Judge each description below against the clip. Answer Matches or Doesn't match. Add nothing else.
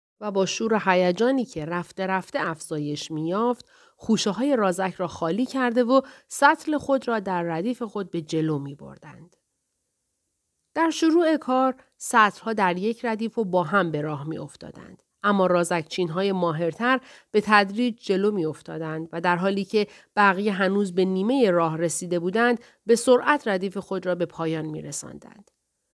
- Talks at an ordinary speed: Doesn't match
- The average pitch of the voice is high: Matches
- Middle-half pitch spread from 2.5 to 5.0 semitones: Doesn't match